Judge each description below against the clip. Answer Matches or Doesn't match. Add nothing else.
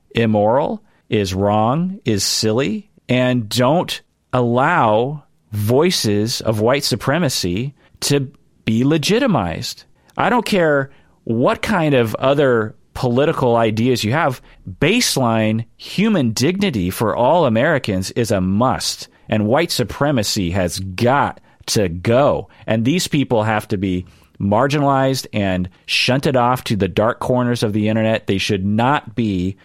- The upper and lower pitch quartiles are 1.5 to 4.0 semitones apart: Doesn't match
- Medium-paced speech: Doesn't match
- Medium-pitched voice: Doesn't match